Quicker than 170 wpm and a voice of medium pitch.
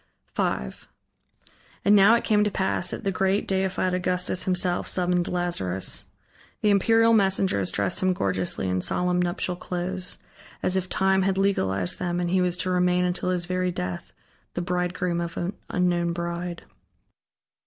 No: average, 155 wpm; medium, 180 Hz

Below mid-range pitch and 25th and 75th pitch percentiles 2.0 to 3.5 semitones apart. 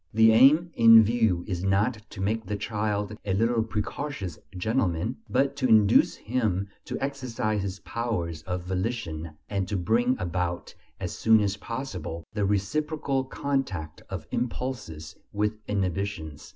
No: low, 105 Hz; average, 4.2 semitones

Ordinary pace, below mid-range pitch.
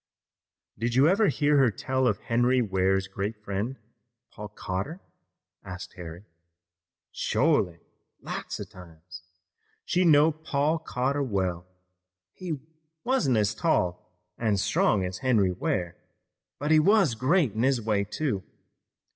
No: slow, 130 wpm; low, 115 Hz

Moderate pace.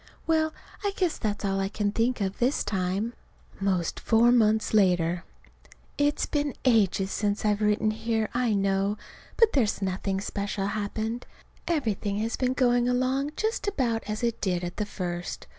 Yes: average, 160 wpm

